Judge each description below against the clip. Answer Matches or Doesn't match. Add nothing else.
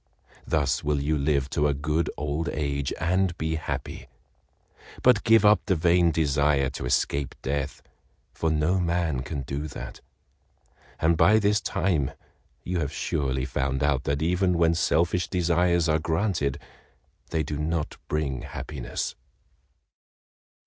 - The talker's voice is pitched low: Matches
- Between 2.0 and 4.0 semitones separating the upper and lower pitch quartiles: Matches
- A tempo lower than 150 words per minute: Matches